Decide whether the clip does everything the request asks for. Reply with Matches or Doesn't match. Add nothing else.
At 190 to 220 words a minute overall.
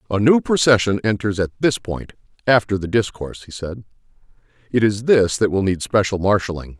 Doesn't match